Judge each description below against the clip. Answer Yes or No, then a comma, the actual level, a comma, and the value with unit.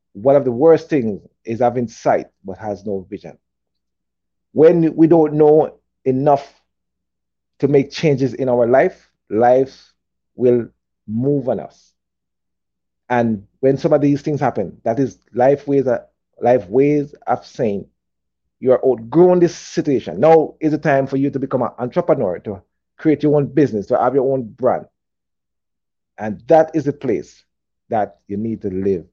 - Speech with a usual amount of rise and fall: No, wide, 6.5 semitones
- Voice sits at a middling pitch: No, low, 130 Hz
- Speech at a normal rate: Yes, average, 165 wpm